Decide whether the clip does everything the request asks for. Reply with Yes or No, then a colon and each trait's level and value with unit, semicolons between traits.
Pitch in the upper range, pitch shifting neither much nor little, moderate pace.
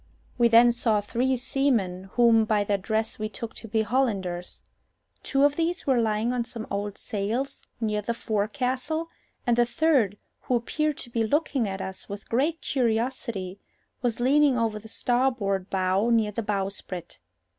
Yes: high, 230 Hz; average, 3.6 semitones; average, 165 wpm